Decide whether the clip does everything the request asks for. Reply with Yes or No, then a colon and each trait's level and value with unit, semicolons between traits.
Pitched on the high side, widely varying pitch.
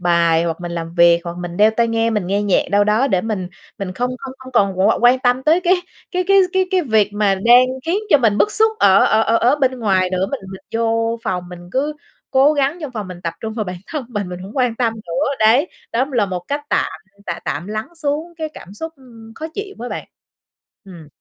Yes: high, 220 Hz; wide, 6.1 semitones